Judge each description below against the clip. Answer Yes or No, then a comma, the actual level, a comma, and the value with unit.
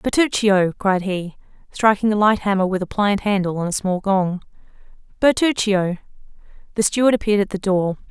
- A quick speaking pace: No, average, 165 wpm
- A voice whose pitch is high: Yes, high, 200 Hz